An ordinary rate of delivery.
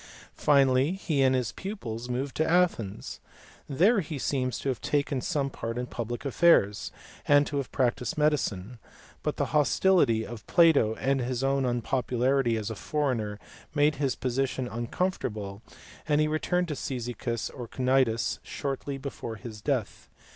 Yes: average, 150 wpm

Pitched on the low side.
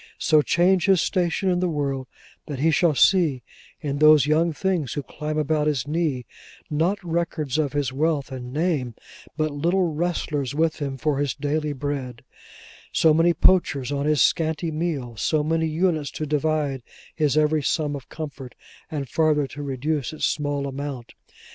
No: medium, 150 Hz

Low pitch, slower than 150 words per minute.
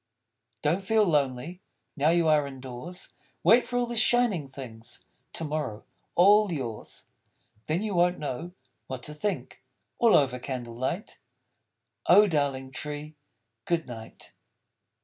No: medium, 150 Hz; average, 140 wpm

